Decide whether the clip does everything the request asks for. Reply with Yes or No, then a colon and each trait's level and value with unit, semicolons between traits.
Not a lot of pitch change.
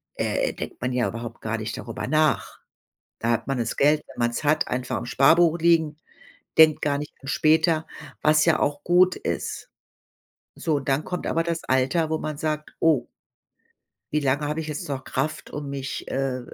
No: average, 3.3 semitones